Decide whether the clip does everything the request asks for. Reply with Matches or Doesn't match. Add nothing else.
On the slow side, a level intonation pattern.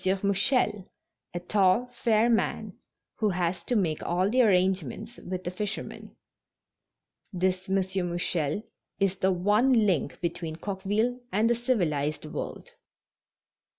Doesn't match